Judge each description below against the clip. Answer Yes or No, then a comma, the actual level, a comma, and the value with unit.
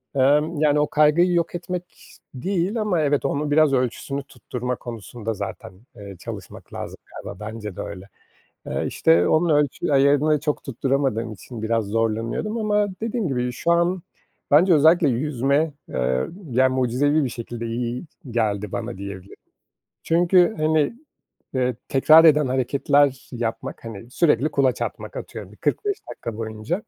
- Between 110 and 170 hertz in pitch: Yes, low, 135 Hz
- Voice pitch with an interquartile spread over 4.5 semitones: Yes, average, 5.2 semitones